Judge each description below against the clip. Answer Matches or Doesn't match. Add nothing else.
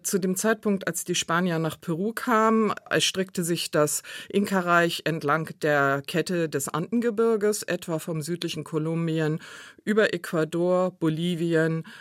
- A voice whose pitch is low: Doesn't match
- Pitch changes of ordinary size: Matches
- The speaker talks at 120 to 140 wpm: Matches